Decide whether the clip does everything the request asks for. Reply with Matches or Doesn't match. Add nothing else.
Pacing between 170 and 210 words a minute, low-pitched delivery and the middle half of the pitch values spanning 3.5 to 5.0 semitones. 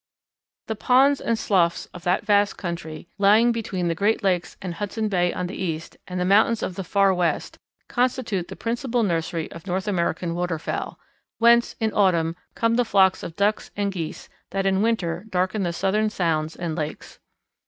Doesn't match